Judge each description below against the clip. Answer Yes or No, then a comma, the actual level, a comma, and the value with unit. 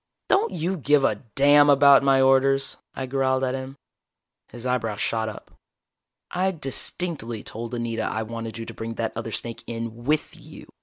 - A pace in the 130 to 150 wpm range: No, average, 170 wpm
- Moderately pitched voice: No, low, 130 Hz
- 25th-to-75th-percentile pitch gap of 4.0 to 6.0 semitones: No, average, 3.6 semitones